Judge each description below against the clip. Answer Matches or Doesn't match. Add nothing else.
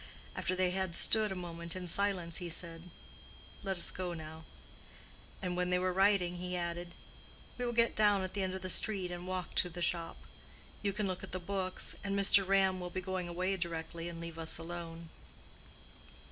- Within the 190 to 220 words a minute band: Matches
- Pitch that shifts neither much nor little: Doesn't match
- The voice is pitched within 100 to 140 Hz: Doesn't match